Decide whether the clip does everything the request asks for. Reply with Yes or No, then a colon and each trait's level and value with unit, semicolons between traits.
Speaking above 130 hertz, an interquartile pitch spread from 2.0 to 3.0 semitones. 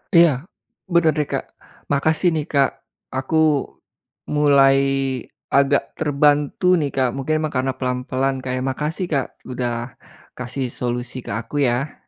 Yes: medium, 140 Hz; narrow, 2.6 semitones